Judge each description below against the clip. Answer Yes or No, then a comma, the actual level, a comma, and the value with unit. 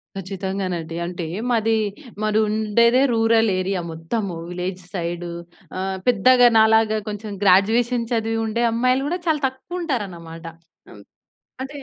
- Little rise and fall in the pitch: No, average, 3.9 semitones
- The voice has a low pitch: No, high, 215 Hz